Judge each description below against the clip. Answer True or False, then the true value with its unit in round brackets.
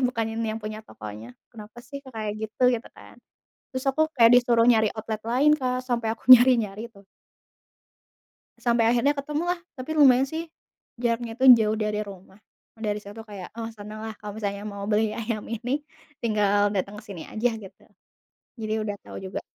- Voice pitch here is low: False (225 Hz)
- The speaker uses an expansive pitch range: False (3.0 semitones)